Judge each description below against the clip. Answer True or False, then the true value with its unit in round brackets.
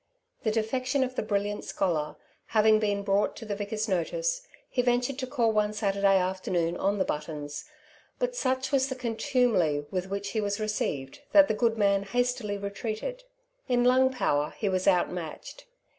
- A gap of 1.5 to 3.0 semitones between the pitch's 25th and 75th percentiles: False (4.3 semitones)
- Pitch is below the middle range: False (215 Hz)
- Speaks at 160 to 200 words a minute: True (170 wpm)